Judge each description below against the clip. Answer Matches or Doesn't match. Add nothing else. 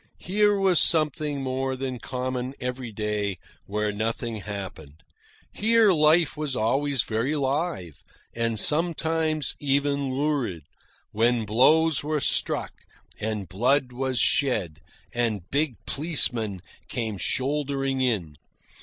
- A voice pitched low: Matches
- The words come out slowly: Matches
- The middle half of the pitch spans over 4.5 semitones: Matches